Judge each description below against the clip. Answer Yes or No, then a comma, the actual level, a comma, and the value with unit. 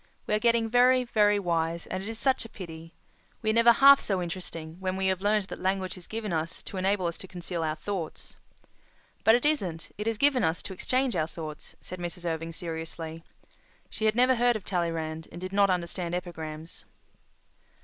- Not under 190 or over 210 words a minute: Yes, average, 200 wpm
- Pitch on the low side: No, medium, 185 Hz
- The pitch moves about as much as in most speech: Yes, average, 4.7 semitones